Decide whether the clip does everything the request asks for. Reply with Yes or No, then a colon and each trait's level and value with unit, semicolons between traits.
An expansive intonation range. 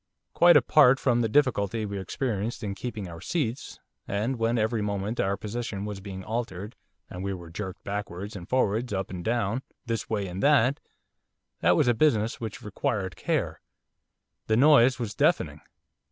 No: average, 3.5 semitones